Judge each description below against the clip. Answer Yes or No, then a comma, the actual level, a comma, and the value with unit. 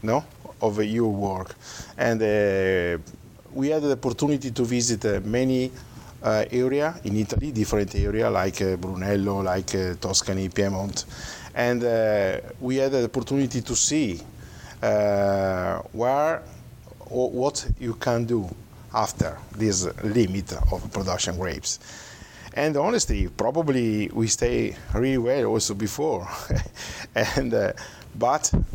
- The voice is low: Yes, low, 110 Hz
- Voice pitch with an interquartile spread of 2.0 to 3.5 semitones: No, average, 3.9 semitones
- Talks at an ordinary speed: No, slow, 125 wpm